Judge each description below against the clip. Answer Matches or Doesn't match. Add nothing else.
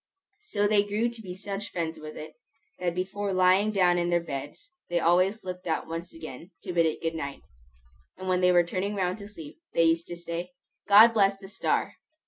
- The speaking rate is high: Matches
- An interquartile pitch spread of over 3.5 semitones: Doesn't match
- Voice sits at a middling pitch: Matches